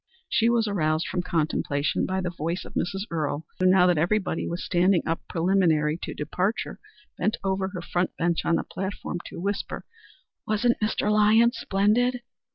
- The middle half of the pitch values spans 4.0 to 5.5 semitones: No, average, 3.6 semitones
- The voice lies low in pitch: No, medium, 185 Hz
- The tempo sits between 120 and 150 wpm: No, average, 165 wpm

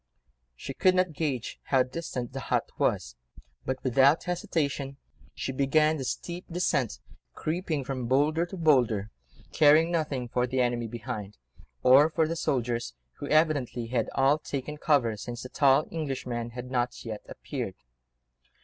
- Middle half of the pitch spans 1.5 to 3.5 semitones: No, average, 4.0 semitones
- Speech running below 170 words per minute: Yes, average, 150 wpm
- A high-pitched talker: No, low, 135 Hz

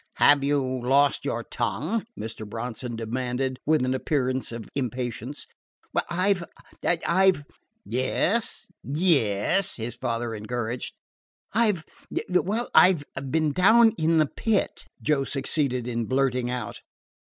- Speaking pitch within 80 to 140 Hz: Yes, low, 135 Hz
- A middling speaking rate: No, slow, 130 wpm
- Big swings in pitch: Yes, wide, 5.7 semitones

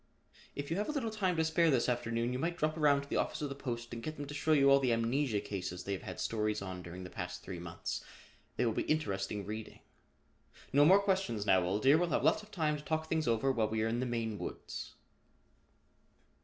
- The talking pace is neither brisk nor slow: No, fast, 245 wpm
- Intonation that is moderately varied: No, wide, 6.3 semitones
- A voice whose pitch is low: Yes, low, 130 Hz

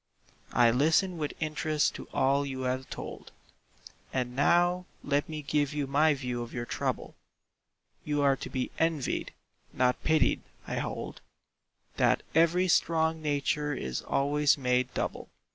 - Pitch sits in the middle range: Yes, medium, 145 Hz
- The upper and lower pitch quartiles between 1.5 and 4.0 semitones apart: Yes, average, 3.3 semitones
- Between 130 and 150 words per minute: Yes, average, 145 wpm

